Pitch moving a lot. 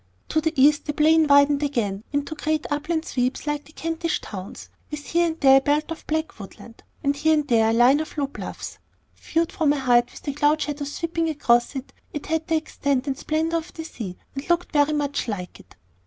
No: average, 2.7 semitones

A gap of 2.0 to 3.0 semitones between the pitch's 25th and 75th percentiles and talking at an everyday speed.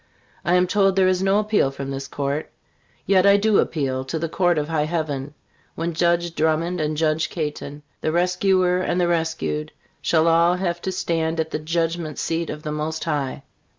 Yes: average, 2.7 semitones; average, 190 wpm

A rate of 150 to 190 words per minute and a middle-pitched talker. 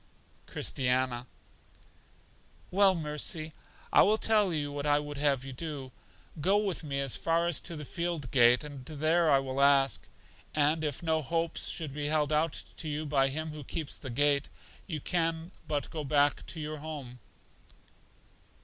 Yes: average, 165 wpm; medium, 150 Hz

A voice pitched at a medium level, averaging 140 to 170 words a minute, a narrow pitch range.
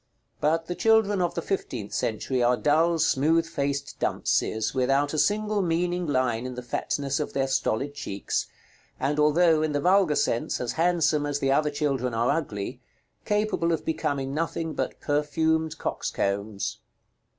No: medium, 150 Hz; average, 155 wpm; average, 3.9 semitones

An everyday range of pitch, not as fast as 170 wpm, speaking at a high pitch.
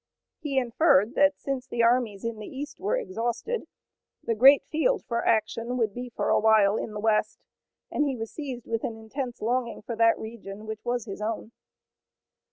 No: average, 3.5 semitones; average, 185 wpm; high, 235 Hz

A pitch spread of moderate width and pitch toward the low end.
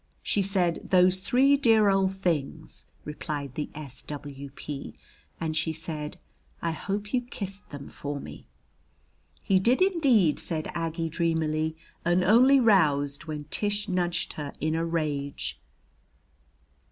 No: average, 4.7 semitones; medium, 165 Hz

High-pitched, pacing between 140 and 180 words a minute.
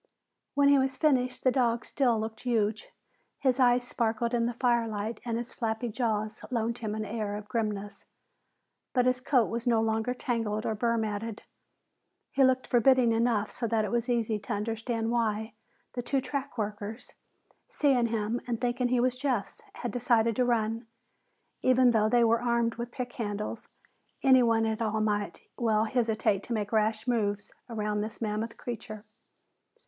Yes: high, 230 Hz; average, 170 wpm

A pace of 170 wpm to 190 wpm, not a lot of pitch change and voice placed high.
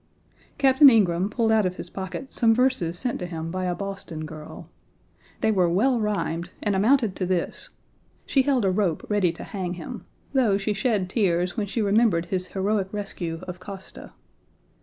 No: average, 180 wpm; average, 3.8 semitones; high, 195 Hz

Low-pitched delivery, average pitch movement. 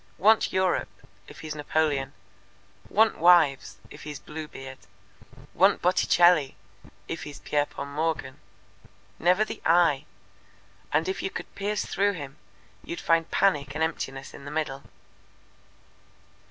No: medium, 160 Hz; average, 4.0 semitones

